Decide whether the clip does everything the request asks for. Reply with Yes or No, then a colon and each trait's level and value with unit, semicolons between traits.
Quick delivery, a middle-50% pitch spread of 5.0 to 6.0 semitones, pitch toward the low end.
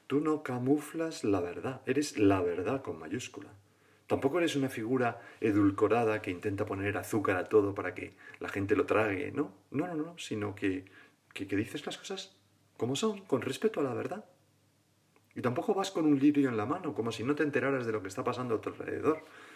Yes: fast, 205 wpm; wide, 5.6 semitones; low, 130 Hz